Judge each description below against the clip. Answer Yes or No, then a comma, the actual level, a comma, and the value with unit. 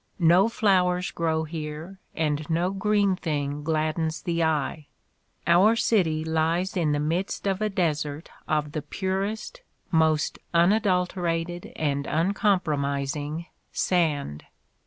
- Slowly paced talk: Yes, slow, 125 wpm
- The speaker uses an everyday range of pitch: Yes, average, 3.6 semitones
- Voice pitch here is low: No, medium, 165 Hz